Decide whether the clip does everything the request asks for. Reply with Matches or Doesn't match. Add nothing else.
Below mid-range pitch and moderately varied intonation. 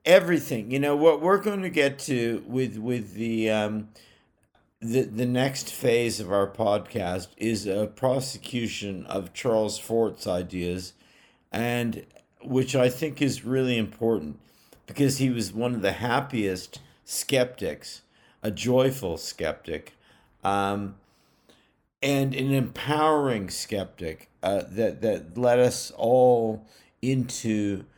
Matches